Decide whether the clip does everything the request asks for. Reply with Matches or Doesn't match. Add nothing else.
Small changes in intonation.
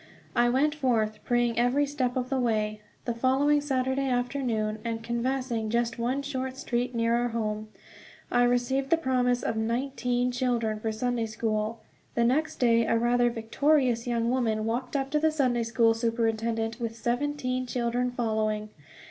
Matches